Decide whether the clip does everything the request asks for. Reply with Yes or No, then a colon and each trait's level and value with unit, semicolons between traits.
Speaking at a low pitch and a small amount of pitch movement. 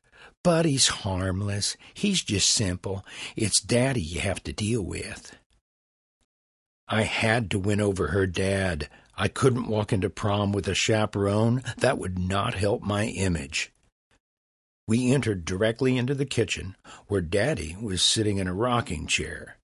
No: low, 100 Hz; average, 4.1 semitones